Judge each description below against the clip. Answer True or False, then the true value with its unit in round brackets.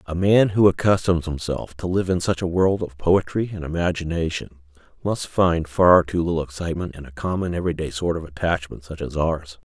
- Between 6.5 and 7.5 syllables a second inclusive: False (5.4 syllables/s)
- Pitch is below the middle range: True (85 Hz)